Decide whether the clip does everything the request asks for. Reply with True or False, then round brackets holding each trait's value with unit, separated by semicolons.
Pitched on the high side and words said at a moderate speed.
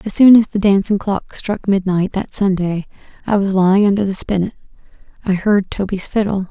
True (195 Hz; 165 wpm)